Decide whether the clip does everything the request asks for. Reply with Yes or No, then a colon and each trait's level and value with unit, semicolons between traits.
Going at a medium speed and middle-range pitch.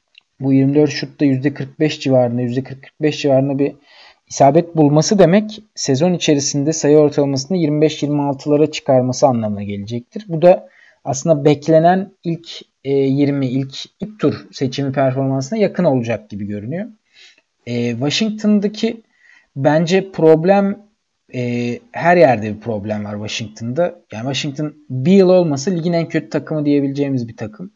Yes: average, 125 wpm; medium, 145 Hz